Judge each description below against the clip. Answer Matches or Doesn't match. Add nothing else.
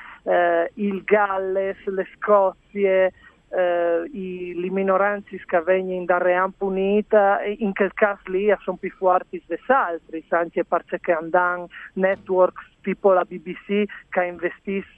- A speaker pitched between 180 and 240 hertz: Matches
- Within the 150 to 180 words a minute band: Doesn't match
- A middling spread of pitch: Doesn't match